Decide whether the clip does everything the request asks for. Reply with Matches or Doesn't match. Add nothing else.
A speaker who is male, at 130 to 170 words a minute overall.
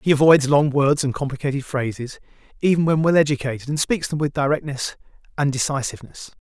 Matches